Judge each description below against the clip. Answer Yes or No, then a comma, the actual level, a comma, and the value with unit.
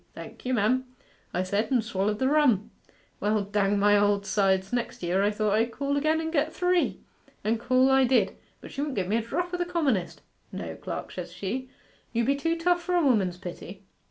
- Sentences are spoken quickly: Yes, fast, 215 wpm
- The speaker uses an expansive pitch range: Yes, wide, 5.8 semitones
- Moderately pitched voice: No, high, 235 Hz